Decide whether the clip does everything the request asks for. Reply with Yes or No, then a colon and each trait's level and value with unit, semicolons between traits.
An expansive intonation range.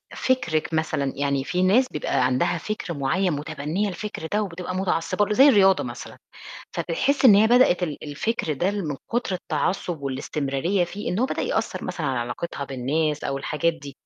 Yes: wide, 5.9 semitones